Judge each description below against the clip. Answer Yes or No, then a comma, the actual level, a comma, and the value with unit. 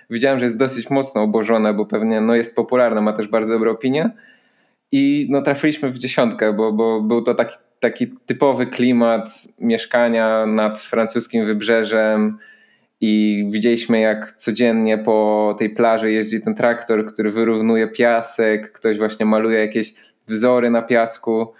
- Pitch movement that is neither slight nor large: No, narrow, 2.0 semitones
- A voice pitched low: Yes, low, 115 Hz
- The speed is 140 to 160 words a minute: Yes, average, 145 wpm